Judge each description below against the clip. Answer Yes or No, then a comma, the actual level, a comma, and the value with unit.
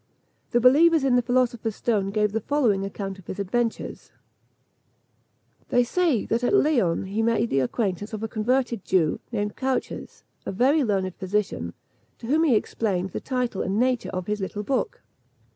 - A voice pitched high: Yes, high, 225 Hz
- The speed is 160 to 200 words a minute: Yes, average, 170 wpm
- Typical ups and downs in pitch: Yes, average, 4.3 semitones